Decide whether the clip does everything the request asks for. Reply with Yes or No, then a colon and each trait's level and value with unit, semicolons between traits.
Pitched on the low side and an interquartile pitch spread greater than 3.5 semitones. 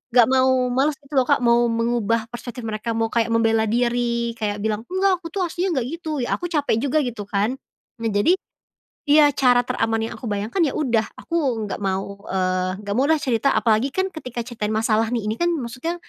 No: high, 240 Hz; average, 4.0 semitones